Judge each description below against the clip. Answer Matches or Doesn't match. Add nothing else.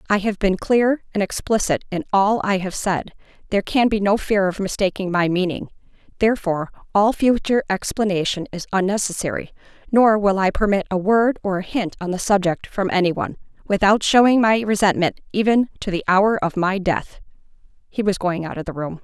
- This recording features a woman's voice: Matches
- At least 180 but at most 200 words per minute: Matches